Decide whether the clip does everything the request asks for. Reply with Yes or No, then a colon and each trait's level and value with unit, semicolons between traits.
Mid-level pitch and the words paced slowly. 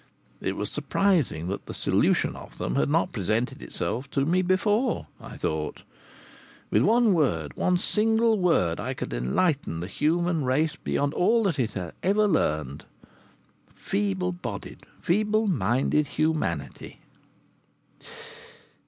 Yes: medium, 150 Hz; slow, 130 wpm